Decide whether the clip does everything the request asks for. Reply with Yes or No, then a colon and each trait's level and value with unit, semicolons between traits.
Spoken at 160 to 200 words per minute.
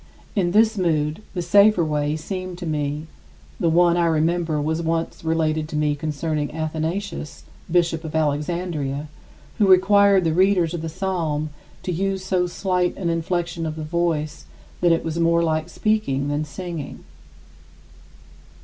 No: average, 150 wpm